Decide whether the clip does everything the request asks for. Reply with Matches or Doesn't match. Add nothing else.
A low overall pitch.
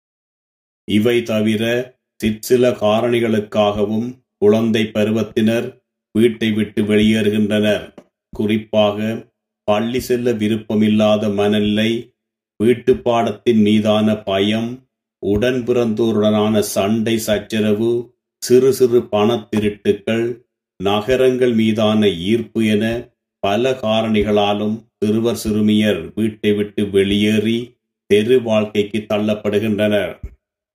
Matches